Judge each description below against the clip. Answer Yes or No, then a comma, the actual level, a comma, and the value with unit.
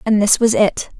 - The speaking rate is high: Yes, fast, 240 wpm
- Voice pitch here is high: Yes, high, 215 Hz